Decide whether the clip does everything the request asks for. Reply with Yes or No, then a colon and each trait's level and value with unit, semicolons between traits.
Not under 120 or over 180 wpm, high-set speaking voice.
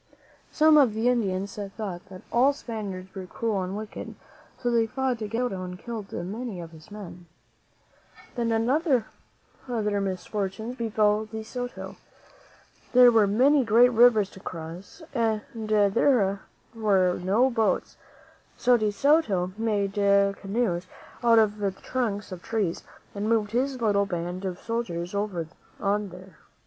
Yes: average, 145 wpm; high, 210 Hz